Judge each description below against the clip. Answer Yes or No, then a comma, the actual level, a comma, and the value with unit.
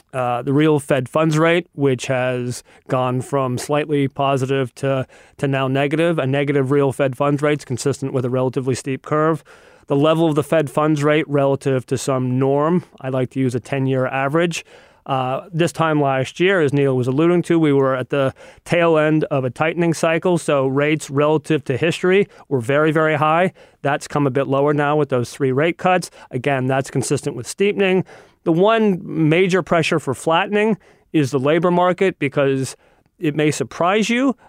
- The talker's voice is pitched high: No, medium, 145 Hz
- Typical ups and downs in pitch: Yes, average, 3.3 semitones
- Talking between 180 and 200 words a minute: Yes, average, 190 wpm